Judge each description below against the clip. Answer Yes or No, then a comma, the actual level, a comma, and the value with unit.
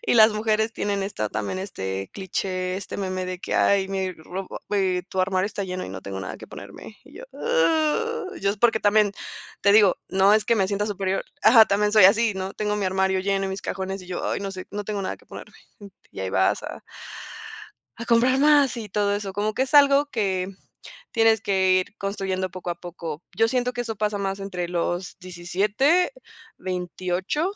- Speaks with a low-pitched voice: No, high, 195 Hz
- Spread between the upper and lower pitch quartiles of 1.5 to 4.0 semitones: Yes, average, 2.9 semitones